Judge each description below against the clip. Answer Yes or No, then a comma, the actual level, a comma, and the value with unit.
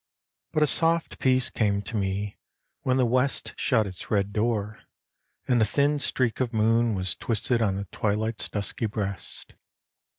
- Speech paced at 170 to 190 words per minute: No, average, 160 wpm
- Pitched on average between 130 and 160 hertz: No, low, 110 Hz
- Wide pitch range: No, average, 3.8 semitones